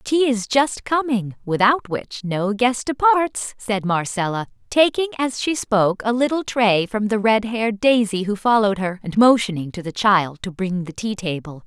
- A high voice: Yes, high, 215 Hz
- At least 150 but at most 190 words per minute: Yes, average, 185 wpm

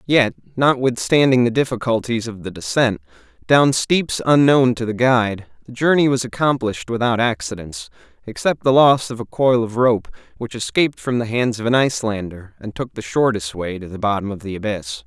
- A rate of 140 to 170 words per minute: No, average, 185 wpm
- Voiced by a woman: No, male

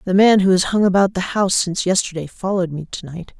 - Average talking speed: No, fast, 245 wpm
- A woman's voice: Yes, female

